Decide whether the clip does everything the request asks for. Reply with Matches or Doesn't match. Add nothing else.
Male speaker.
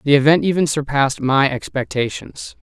Matches